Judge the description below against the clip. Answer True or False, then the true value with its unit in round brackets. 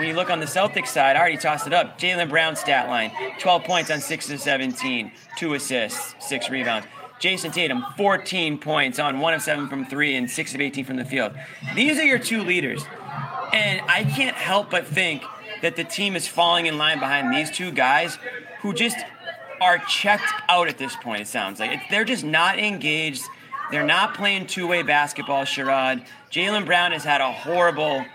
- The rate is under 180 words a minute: False (200 wpm)